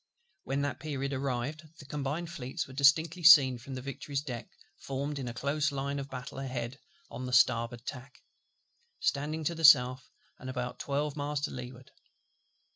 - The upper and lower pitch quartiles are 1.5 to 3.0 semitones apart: Yes, narrow, 2.5 semitones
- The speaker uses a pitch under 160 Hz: Yes, medium, 140 Hz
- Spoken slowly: No, average, 170 wpm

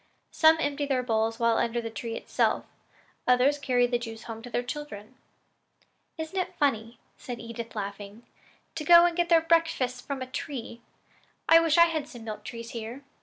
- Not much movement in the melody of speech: No, average, 4.6 semitones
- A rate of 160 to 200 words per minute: Yes, average, 180 wpm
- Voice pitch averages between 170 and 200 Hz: No, very high, 250 Hz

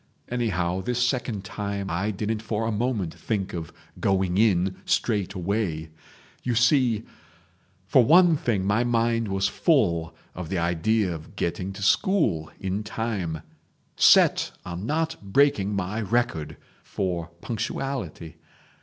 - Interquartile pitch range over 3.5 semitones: Yes, average, 4.4 semitones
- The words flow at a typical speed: No, slow, 130 wpm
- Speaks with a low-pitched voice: Yes, low, 100 Hz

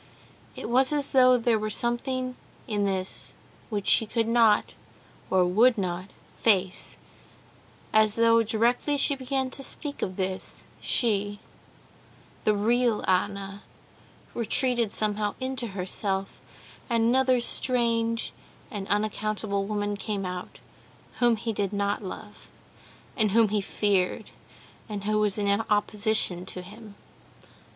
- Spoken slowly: Yes, slow, 125 wpm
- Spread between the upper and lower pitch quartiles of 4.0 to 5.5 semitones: No, average, 2.9 semitones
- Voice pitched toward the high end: Yes, high, 215 Hz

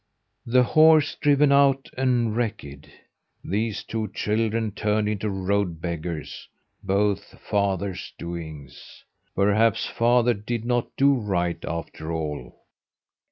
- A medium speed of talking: No, slow, 110 wpm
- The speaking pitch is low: Yes, low, 105 Hz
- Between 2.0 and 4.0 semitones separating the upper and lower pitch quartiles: No, average, 5.3 semitones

